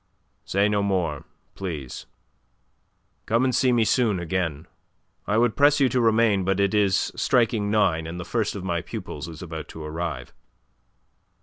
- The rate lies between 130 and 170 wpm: Yes, average, 165 wpm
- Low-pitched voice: Yes, low, 100 Hz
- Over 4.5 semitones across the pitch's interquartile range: Yes, average, 4.9 semitones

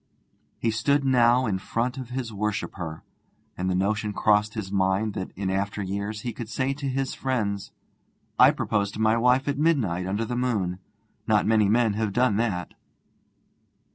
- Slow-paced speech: No, average, 170 wpm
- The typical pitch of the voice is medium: No, low, 110 Hz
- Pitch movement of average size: Yes, average, 3.7 semitones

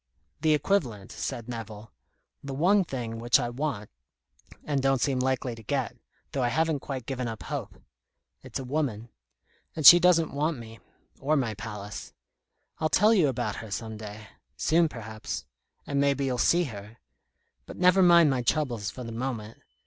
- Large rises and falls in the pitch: No, average, 5.0 semitones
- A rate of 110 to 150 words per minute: No, average, 170 wpm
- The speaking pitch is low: Yes, low, 130 Hz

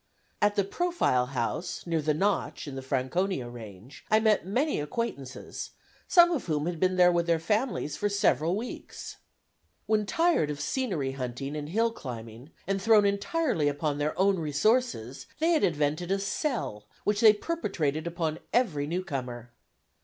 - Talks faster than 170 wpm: No, average, 160 wpm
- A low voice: No, medium, 170 Hz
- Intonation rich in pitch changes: Yes, wide, 6.6 semitones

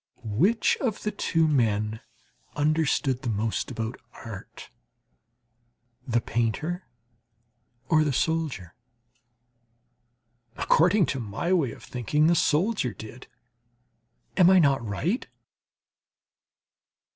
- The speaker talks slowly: Yes, slow, 100 wpm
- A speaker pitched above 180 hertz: No, medium, 140 Hz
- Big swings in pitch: Yes, wide, 6.8 semitones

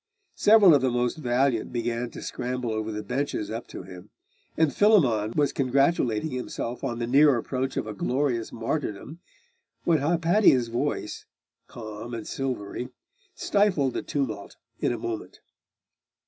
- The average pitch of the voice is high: No, low, 125 Hz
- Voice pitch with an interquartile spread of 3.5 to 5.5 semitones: Yes, average, 3.9 semitones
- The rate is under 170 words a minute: Yes, average, 145 wpm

